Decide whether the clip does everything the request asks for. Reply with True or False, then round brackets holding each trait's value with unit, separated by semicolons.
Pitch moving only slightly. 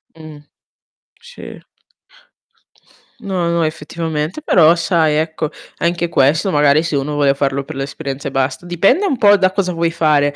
False (3.2 semitones)